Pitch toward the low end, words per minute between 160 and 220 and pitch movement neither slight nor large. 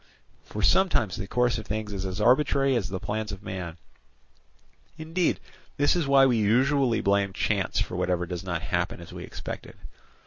No: low, 105 Hz; average, 175 wpm; wide, 6.0 semitones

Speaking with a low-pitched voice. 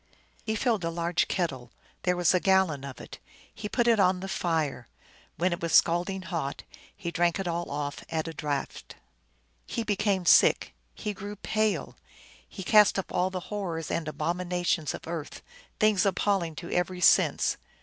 No: medium, 180 Hz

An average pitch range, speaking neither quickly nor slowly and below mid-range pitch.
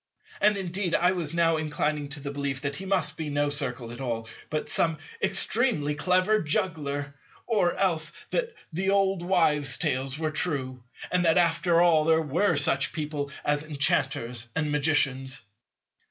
No: average, 3.8 semitones; average, 160 wpm; medium, 155 Hz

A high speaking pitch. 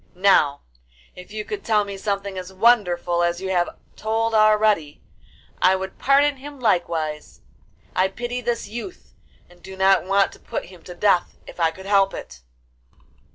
Yes: high, 195 Hz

